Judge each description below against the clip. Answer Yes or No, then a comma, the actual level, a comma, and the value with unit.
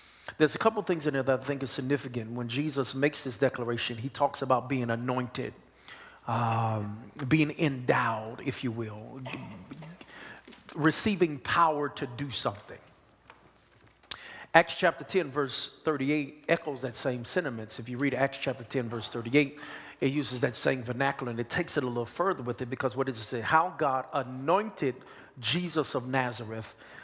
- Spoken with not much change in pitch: No, average, 3.4 semitones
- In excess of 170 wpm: No, average, 165 wpm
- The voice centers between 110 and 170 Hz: Yes, low, 135 Hz